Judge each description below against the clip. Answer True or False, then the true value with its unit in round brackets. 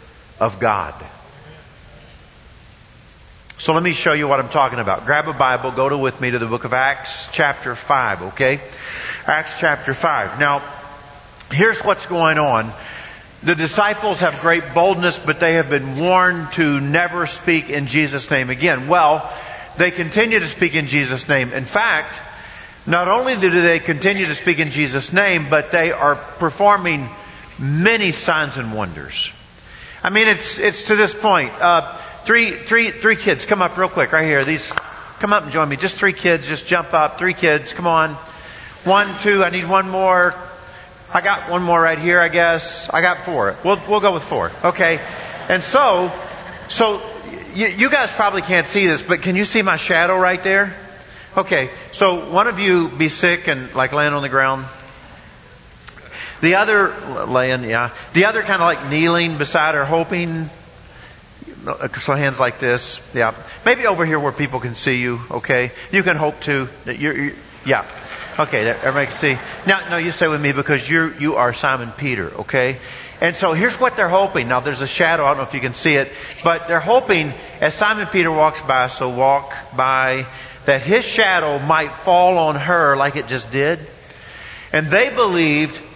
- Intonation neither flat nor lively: True (4.6 semitones)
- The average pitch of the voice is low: False (160 Hz)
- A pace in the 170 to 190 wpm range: True (180 wpm)